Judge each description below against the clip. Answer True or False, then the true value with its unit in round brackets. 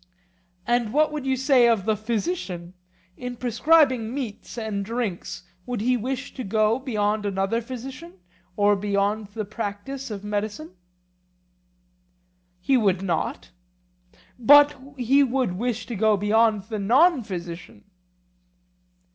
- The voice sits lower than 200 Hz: False (220 Hz)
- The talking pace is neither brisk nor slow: False (125 wpm)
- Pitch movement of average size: True (3.9 semitones)